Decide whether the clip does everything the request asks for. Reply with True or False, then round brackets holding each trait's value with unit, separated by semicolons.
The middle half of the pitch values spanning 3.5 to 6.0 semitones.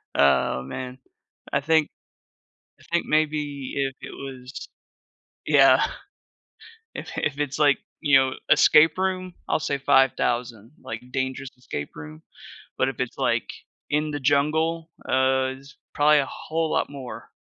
False (2.7 semitones)